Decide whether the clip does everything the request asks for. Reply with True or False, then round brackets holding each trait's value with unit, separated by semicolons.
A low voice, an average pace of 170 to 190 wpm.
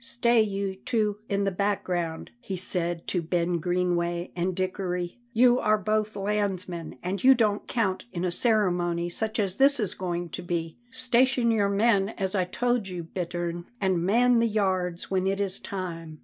False (190 Hz; 175 wpm)